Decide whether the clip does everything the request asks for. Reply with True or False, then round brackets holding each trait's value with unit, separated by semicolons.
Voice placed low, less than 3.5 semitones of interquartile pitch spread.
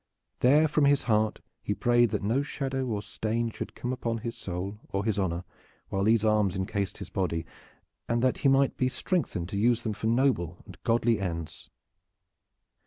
False (110 Hz; 4.0 semitones)